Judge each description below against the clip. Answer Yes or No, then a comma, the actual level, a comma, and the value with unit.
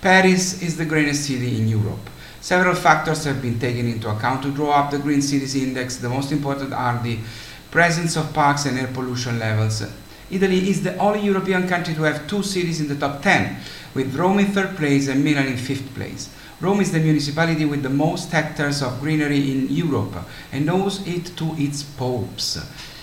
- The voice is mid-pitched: Yes, medium, 145 Hz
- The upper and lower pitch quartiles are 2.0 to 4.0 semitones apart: No, average, 4.4 semitones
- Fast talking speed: No, average, 195 wpm